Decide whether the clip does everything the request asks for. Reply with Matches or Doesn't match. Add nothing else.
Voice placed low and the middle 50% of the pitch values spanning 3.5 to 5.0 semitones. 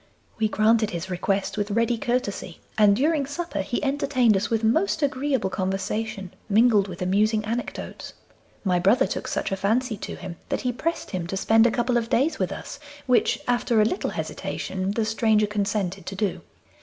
Doesn't match